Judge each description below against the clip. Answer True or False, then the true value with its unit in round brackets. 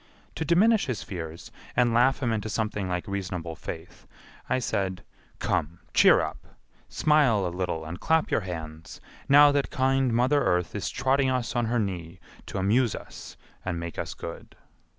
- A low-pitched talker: True (105 Hz)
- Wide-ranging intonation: True (6.7 semitones)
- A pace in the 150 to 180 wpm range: True (170 wpm)